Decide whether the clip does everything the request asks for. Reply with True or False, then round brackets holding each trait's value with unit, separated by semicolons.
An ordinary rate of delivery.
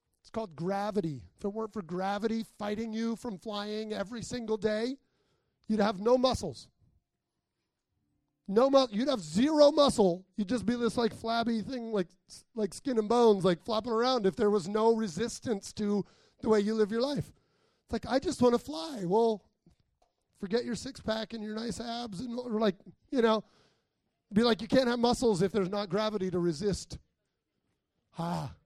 True (180 wpm)